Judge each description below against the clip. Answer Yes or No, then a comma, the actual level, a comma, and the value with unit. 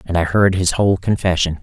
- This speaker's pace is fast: Yes, fast, 220 wpm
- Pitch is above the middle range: No, very low, 90 Hz